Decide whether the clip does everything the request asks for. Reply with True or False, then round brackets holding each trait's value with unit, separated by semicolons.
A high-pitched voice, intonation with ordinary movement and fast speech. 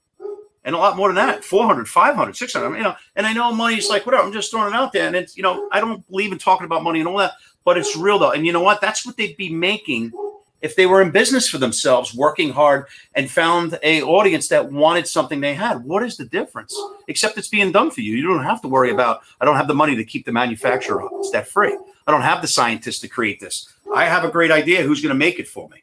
False (200 Hz; 6.5 semitones; 270 wpm)